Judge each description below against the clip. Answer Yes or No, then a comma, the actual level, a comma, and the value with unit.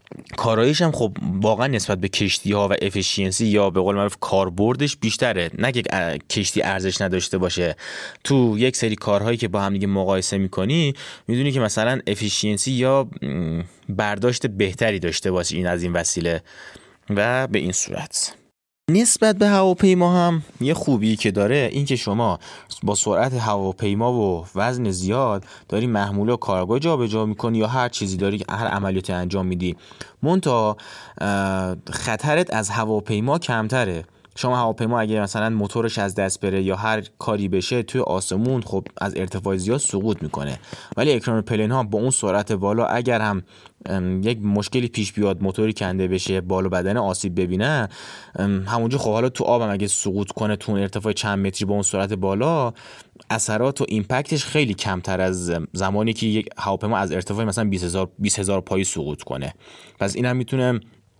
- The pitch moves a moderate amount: Yes, average, 3.6 semitones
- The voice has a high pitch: No, low, 105 Hz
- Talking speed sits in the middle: No, fast, 165 wpm